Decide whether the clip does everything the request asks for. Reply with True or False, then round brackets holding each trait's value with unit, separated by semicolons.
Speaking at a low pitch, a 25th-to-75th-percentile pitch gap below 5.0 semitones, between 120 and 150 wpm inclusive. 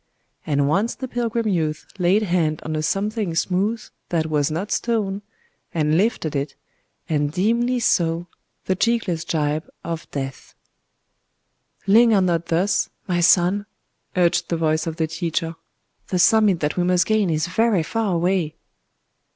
False (175 Hz; 4.5 semitones; 135 wpm)